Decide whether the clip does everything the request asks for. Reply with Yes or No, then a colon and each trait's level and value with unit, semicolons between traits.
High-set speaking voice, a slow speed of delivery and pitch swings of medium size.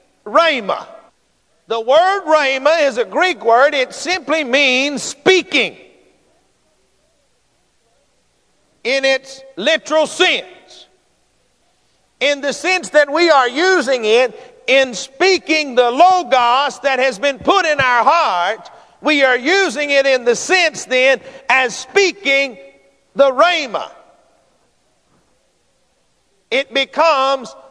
Yes: very high, 275 Hz; slow, 105 wpm; average, 3.5 semitones